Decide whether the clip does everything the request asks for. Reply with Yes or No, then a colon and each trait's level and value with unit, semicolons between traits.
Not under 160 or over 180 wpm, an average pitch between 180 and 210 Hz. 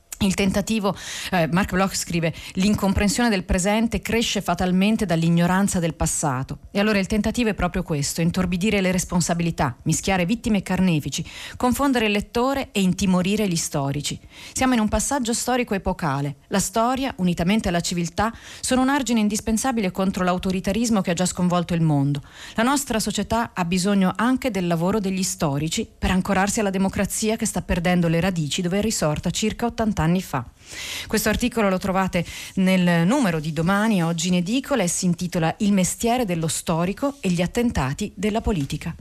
Yes: average, 165 wpm; high, 190 Hz